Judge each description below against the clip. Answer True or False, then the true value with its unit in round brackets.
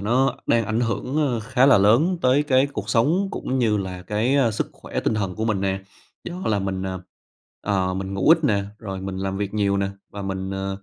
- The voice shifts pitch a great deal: False (4.5 semitones)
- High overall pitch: False (105 Hz)